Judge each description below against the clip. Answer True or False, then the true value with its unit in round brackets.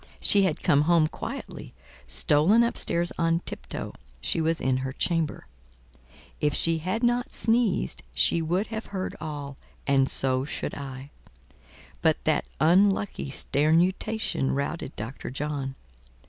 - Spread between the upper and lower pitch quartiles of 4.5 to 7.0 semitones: True (5.1 semitones)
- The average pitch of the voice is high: False (160 Hz)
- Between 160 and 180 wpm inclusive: False (135 wpm)